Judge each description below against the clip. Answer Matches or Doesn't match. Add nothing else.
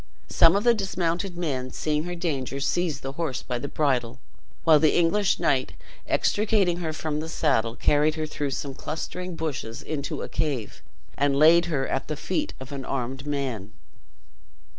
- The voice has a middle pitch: Matches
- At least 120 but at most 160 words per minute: Doesn't match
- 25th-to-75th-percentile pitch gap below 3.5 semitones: Doesn't match